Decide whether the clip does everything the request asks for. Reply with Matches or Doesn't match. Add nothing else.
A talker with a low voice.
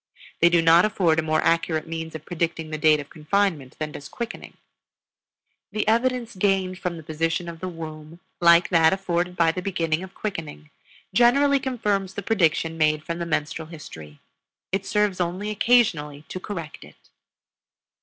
Doesn't match